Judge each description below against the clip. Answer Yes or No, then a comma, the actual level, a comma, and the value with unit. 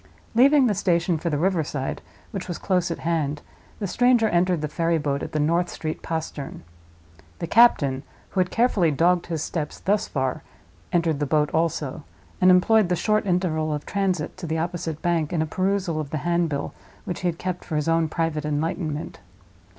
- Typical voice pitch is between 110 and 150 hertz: No, medium, 170 Hz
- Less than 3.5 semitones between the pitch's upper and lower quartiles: Yes, average, 3.0 semitones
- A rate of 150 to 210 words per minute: Yes, average, 190 wpm